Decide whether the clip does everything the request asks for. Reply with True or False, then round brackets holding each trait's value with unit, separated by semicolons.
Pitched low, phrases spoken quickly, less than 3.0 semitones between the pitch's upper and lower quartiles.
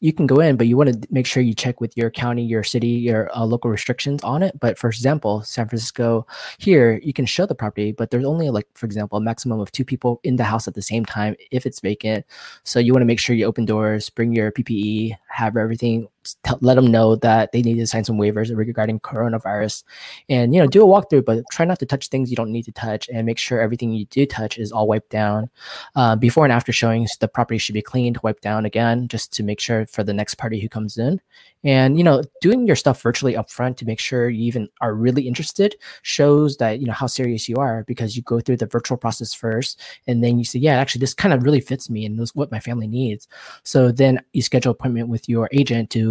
True (115 Hz; 250 wpm; 2.6 semitones)